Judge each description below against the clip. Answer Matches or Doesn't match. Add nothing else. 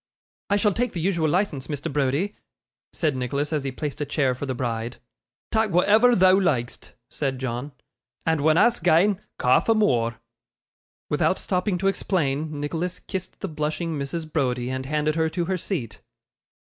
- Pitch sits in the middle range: Matches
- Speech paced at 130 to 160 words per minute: Doesn't match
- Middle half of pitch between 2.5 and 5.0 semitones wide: Doesn't match